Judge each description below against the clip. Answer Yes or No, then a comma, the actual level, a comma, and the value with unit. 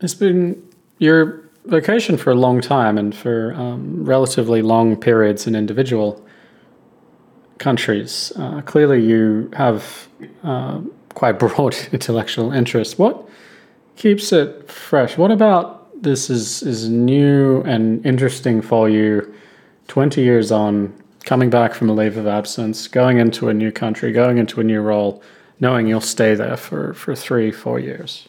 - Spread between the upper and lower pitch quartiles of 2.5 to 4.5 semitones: Yes, average, 3.5 semitones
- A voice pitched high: No, low, 115 Hz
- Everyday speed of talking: Yes, average, 145 wpm